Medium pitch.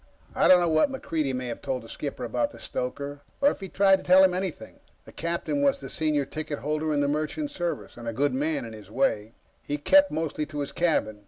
Yes: medium, 155 Hz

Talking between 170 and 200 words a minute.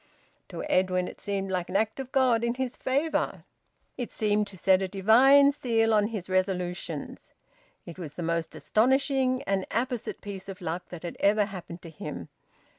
Yes: average, 180 wpm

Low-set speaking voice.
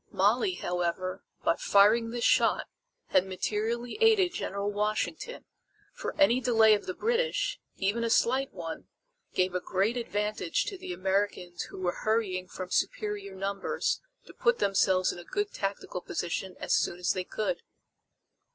No: high, 205 Hz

